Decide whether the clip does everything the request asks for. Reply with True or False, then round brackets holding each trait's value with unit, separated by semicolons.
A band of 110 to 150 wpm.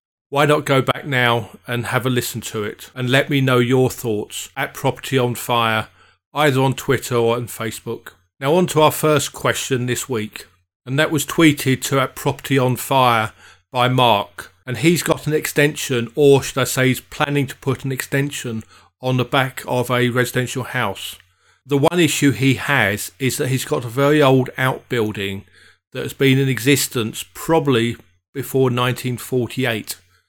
False (180 wpm)